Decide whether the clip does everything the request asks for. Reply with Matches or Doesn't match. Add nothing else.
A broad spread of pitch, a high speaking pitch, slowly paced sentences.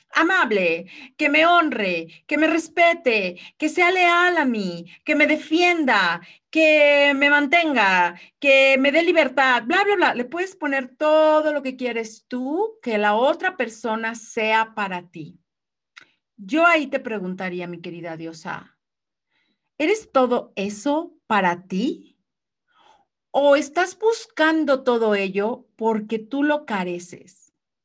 Matches